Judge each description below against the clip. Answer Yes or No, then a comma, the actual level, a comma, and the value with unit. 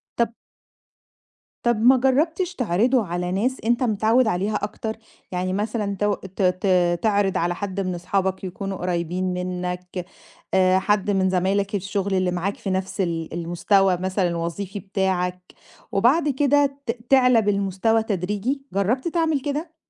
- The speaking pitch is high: Yes, high, 195 Hz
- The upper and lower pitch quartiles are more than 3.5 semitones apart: Yes, average, 4.1 semitones